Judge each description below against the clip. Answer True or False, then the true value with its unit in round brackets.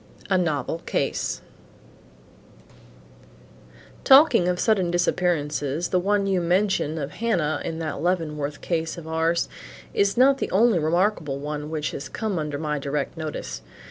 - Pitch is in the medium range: True (165 Hz)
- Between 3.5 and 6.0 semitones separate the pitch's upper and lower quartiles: True (4.0 semitones)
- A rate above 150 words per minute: False (140 wpm)